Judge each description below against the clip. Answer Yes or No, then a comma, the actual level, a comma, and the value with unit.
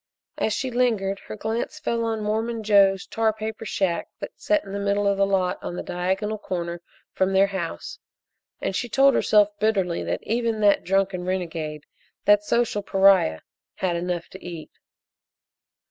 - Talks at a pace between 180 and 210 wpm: No, average, 165 wpm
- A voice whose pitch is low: No, high, 200 Hz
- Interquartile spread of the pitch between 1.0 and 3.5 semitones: Yes, average, 2.9 semitones